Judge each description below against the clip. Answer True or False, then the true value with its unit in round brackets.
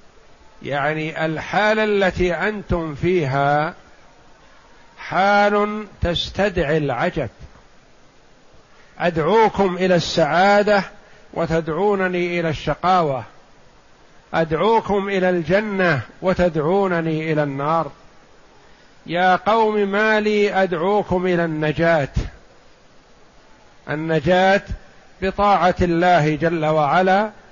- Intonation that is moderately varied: True (3.8 semitones)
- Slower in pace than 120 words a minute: True (70 wpm)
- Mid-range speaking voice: True (180 Hz)